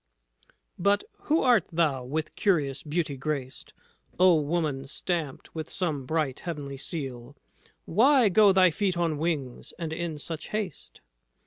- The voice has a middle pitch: Yes, medium, 160 Hz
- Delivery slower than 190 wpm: Yes, slow, 135 wpm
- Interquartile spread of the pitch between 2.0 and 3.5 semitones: No, average, 4.2 semitones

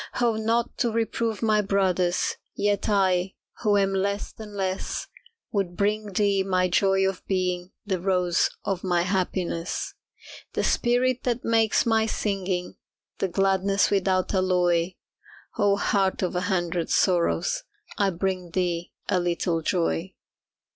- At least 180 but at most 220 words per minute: No, slow, 135 wpm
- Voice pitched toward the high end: Yes, high, 195 Hz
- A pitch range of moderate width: No, narrow, 2.2 semitones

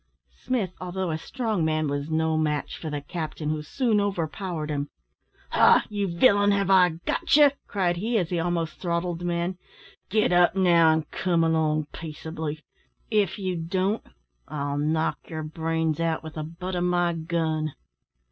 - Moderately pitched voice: Yes, medium, 170 Hz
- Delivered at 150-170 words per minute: Yes, average, 165 wpm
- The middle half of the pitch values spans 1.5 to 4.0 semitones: Yes, average, 2.9 semitones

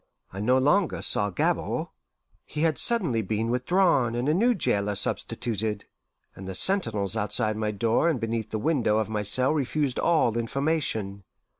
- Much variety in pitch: Yes, wide, 6.2 semitones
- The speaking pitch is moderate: No, low, 115 Hz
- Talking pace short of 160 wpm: No, average, 165 wpm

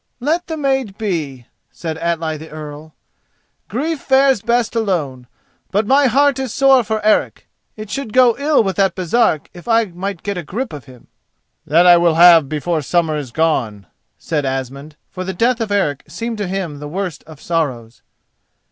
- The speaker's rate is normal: Yes, average, 180 wpm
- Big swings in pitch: Yes, wide, 7.0 semitones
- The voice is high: No, medium, 180 Hz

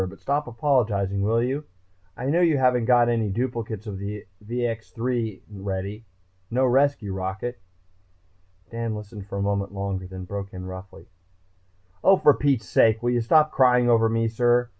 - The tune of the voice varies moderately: Yes, average, 3.7 semitones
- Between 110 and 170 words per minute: Yes, average, 160 wpm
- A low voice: Yes, low, 115 Hz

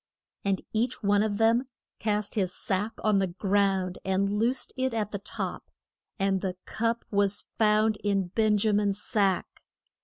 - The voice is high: Yes, high, 205 Hz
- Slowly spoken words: No, average, 160 wpm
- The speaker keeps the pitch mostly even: Yes, narrow, 1.9 semitones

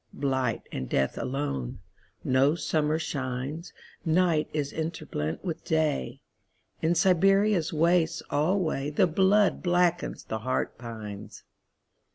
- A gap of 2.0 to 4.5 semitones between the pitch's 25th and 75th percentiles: No, average, 5.0 semitones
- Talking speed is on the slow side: Yes, slow, 90 wpm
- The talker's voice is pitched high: No, medium, 155 Hz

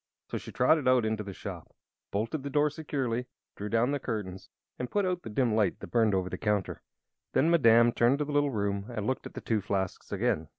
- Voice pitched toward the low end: Yes, low, 115 Hz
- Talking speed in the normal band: No, fast, 230 wpm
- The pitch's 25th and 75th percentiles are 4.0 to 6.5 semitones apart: Yes, average, 5.0 semitones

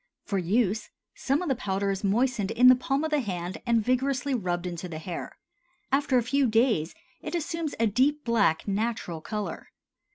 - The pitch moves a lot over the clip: Yes, wide, 5.7 semitones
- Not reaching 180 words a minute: No, average, 185 wpm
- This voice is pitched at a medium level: No, high, 230 Hz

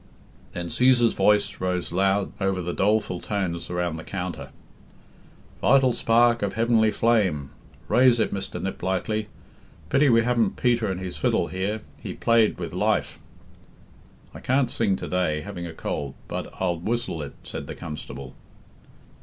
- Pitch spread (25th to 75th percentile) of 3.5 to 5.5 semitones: Yes, average, 4.6 semitones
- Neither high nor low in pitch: No, low, 100 Hz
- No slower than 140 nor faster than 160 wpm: Yes, average, 150 wpm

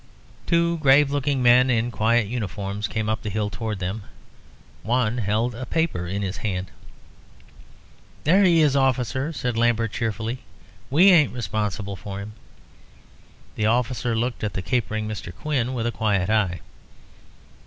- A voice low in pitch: Yes, low, 115 Hz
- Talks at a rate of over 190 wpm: No, average, 150 wpm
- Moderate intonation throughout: Yes, average, 3.6 semitones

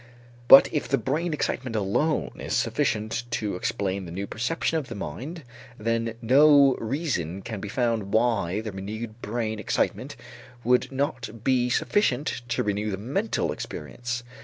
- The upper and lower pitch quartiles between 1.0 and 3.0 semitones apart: No, average, 4.1 semitones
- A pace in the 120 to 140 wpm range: No, average, 150 wpm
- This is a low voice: Yes, low, 115 Hz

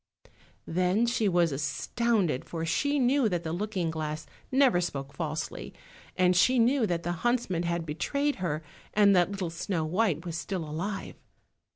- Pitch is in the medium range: Yes, medium, 180 Hz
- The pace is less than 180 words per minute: Yes, average, 160 wpm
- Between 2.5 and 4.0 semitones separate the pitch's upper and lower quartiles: No, average, 5.2 semitones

